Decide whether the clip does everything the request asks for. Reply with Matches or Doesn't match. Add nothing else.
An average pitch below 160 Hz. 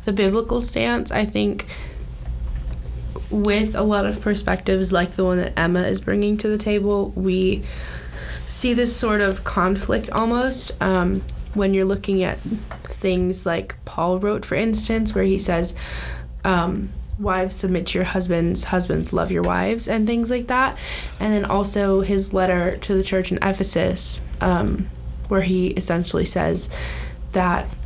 Doesn't match